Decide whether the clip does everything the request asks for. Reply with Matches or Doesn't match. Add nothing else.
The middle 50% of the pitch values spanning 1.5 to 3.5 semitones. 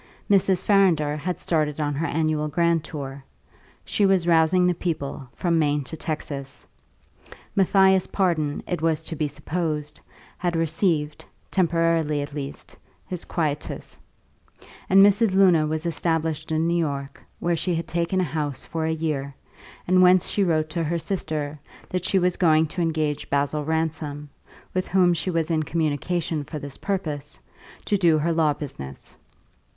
Matches